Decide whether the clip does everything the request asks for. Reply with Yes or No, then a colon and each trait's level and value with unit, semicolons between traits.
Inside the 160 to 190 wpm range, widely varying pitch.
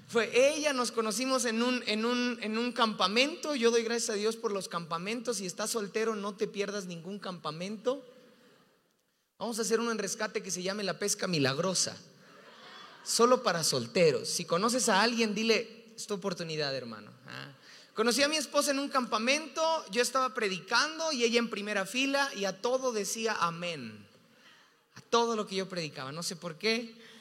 No: average, 175 wpm; average, 3.9 semitones